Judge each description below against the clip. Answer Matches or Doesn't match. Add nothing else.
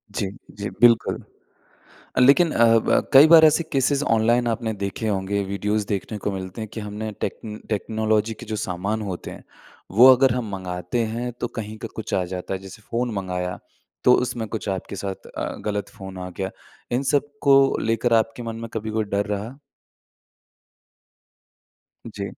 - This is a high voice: Doesn't match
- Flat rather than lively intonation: Doesn't match